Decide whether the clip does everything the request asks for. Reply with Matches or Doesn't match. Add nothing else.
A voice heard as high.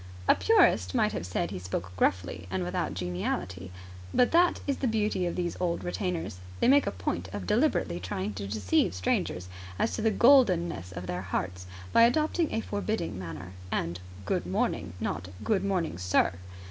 Doesn't match